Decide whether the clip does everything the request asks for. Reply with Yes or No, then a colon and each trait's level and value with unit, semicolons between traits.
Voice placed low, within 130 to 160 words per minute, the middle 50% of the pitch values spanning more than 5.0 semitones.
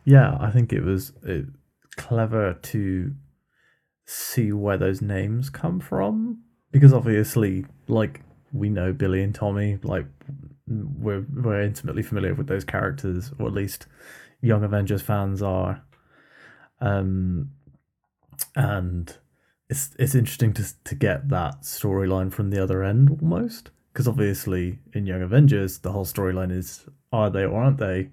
Yes: low, 105 Hz; average, 140 wpm; wide, 5.6 semitones